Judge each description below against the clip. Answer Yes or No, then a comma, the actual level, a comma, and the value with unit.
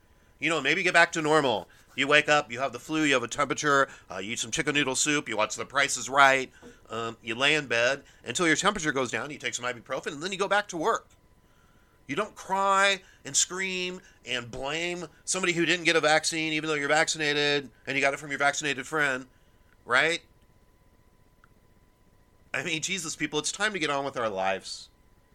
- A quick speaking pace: Yes, fast, 210 wpm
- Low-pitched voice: No, medium, 145 Hz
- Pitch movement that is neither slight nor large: Yes, average, 4.2 semitones